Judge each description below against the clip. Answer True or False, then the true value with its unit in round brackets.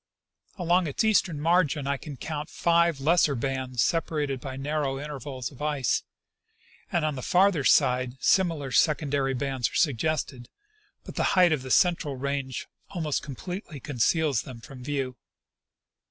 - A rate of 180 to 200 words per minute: False (145 wpm)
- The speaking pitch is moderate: True (145 Hz)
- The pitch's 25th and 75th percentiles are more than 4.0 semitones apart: False (3.4 semitones)